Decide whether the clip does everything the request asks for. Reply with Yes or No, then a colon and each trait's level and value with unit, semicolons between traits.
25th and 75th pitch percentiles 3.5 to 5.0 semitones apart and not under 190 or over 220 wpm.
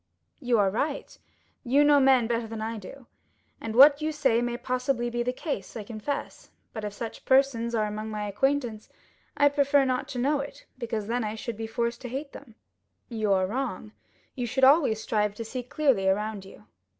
Yes: average, 3.9 semitones; average, 200 wpm